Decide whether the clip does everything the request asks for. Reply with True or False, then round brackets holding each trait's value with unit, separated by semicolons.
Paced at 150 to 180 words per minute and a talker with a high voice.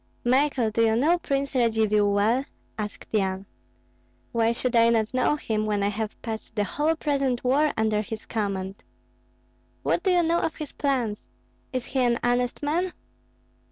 True (165 wpm; 235 Hz)